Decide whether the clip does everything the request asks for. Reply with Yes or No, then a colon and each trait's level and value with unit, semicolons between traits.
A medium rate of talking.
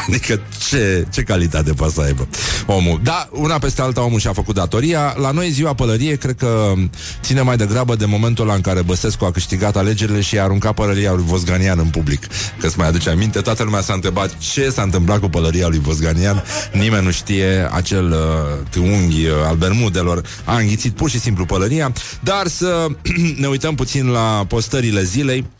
No: fast, 185 wpm